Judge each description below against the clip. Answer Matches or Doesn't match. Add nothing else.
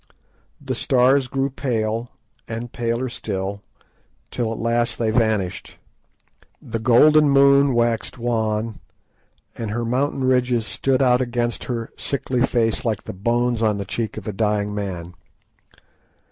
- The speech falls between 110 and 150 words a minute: Matches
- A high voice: Doesn't match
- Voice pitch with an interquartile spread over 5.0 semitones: Doesn't match